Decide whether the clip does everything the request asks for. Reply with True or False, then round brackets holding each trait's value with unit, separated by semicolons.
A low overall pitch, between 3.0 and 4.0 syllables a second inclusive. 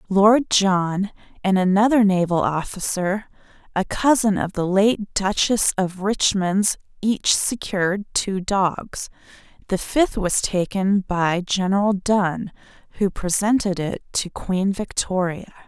False (195 Hz; 3.7 syllables/s)